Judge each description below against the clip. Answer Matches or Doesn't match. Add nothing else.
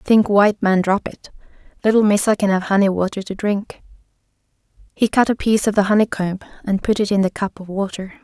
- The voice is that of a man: Doesn't match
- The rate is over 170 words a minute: Matches